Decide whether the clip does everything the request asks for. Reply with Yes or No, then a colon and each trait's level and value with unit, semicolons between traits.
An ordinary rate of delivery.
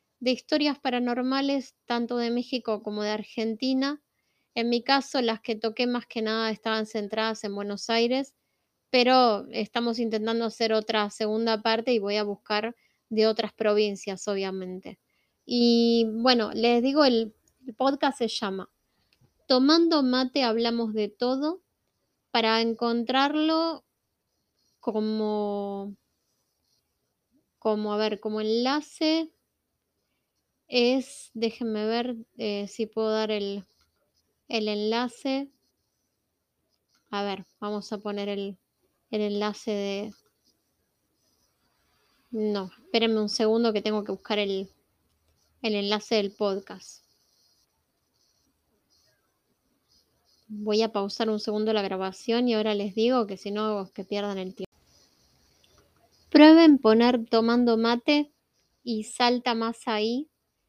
No: slow, 115 wpm